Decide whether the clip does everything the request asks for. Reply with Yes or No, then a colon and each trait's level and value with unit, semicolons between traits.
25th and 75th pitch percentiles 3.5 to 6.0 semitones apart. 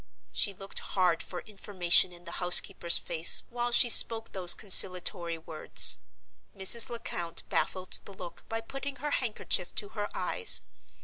Yes: average, 4.3 semitones